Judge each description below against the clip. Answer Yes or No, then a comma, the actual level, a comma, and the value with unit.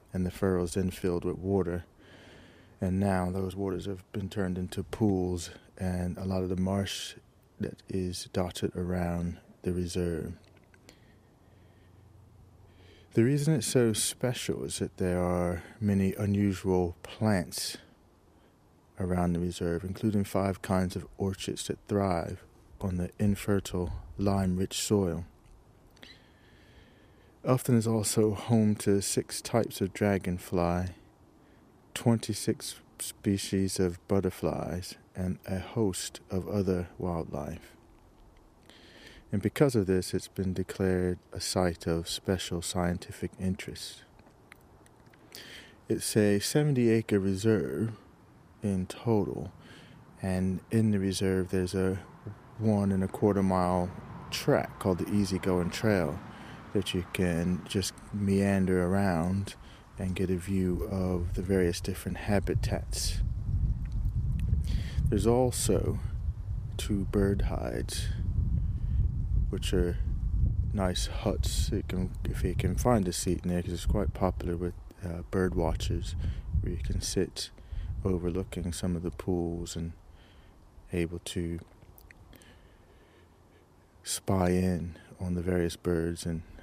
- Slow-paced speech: Yes, slow, 120 wpm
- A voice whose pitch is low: Yes, very low, 95 Hz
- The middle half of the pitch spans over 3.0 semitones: No, narrow, 2.4 semitones